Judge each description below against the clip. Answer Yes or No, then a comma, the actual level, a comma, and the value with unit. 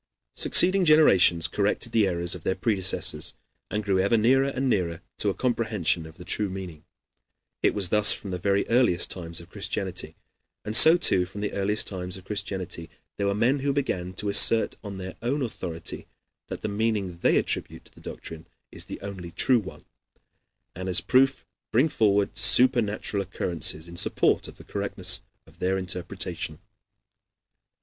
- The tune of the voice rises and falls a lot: No, average, 4.0 semitones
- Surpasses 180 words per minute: No, average, 170 wpm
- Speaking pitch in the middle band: No, low, 100 Hz